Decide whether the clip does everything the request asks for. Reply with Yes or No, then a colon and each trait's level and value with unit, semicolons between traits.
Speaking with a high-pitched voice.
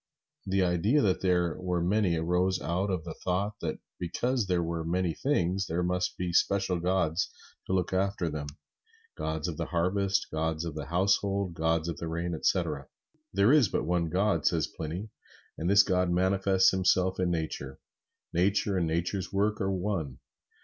No: very low, 90 Hz